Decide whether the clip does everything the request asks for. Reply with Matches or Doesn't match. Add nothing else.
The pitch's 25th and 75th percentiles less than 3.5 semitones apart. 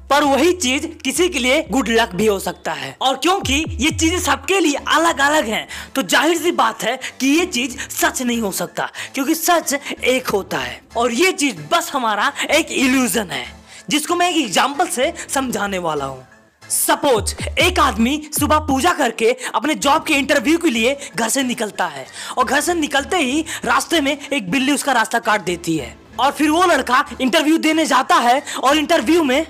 Doesn't match